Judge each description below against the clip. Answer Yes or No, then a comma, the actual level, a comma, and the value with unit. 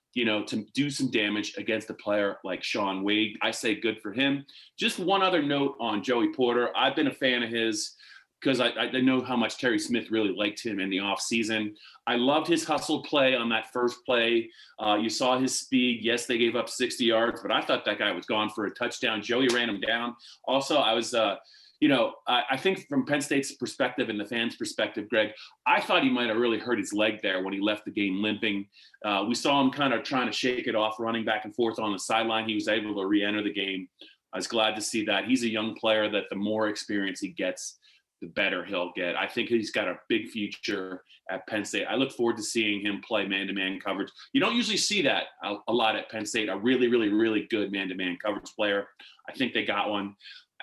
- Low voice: Yes, low, 115 Hz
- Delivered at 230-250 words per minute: Yes, fast, 245 wpm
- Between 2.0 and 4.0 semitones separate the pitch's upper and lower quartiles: Yes, average, 3.6 semitones